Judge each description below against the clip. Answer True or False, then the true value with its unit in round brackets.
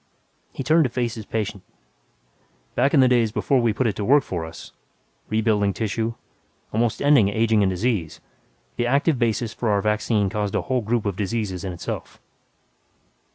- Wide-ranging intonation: False (2.9 semitones)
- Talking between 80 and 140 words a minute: False (175 wpm)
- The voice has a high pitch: False (110 Hz)